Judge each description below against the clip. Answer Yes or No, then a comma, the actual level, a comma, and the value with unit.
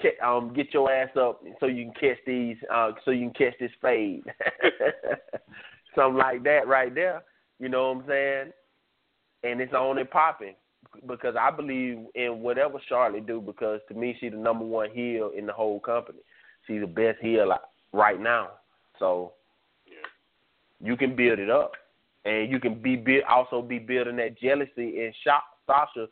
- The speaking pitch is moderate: No, low, 120 Hz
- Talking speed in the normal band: Yes, average, 170 wpm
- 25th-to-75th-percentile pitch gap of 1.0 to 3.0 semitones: Yes, narrow, 2.5 semitones